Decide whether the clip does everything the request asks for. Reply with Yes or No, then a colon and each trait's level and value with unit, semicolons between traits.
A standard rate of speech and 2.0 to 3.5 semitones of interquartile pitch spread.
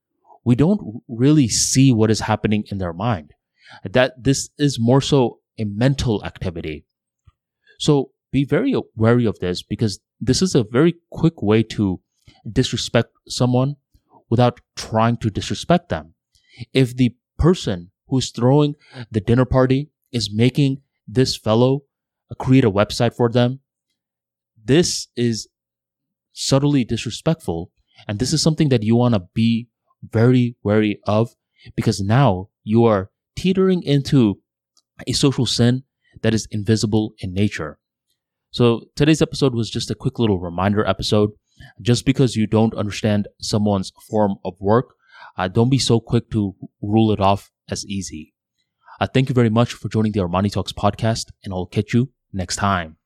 No: average, 150 wpm; average, 3.9 semitones